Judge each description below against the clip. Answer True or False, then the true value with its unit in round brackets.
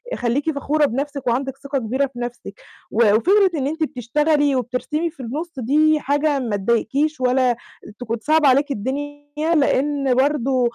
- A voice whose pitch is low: False (275 Hz)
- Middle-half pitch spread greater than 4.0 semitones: False (3.2 semitones)